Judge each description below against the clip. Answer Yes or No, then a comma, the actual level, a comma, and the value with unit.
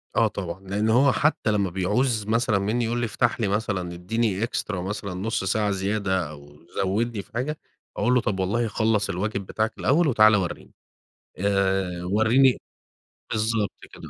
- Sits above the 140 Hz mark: No, low, 105 Hz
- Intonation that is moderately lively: Yes, average, 3.2 semitones